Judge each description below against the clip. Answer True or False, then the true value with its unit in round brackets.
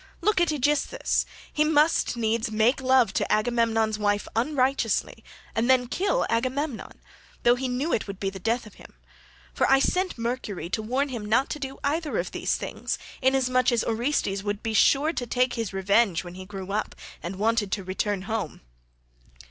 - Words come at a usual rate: True (180 wpm)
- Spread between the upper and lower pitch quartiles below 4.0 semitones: False (4.3 semitones)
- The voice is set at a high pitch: True (235 Hz)